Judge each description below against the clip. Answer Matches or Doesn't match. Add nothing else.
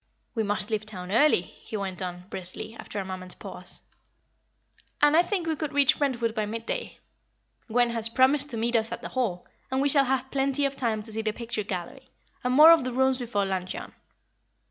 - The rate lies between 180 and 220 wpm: Matches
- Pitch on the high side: Matches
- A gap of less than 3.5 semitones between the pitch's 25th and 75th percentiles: Doesn't match